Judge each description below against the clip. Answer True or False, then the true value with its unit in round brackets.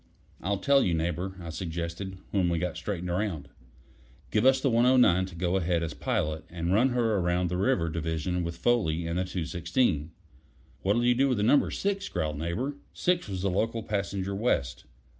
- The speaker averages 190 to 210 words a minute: False (180 wpm)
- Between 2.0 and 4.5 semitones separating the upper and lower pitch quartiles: False (5.1 semitones)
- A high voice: False (95 Hz)